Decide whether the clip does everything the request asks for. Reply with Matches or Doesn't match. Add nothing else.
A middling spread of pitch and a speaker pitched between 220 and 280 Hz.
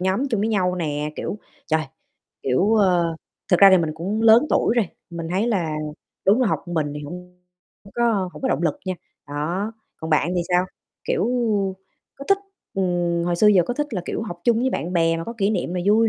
Doesn't match